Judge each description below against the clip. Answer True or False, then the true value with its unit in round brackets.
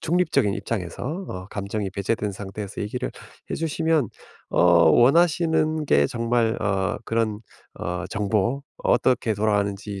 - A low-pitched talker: True (110 Hz)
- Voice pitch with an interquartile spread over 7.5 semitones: False (5.2 semitones)